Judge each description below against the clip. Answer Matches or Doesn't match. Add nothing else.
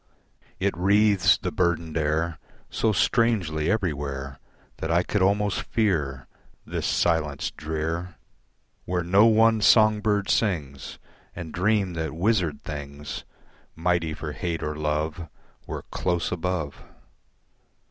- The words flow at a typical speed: Doesn't match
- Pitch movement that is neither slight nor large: Matches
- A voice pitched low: Matches